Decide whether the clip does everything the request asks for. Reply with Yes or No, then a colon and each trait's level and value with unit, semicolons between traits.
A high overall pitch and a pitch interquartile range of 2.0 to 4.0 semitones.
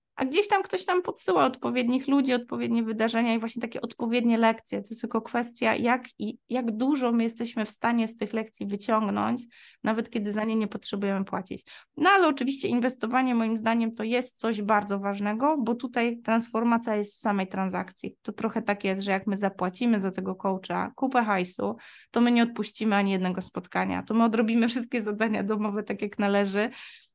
Yes: high, 225 Hz; narrow, 2.6 semitones